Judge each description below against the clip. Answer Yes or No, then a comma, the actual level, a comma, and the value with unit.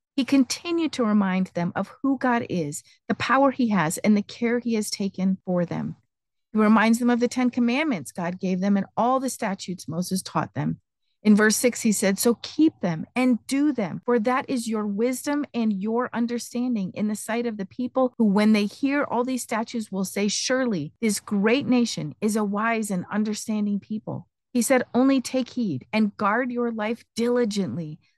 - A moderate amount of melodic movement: Yes, average, 3.7 semitones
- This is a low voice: No, high, 220 Hz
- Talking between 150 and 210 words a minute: Yes, average, 195 wpm